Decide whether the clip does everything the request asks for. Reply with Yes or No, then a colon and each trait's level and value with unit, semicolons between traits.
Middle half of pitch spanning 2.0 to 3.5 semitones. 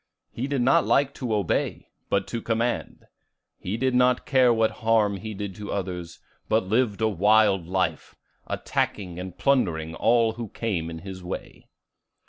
No: average, 4.0 semitones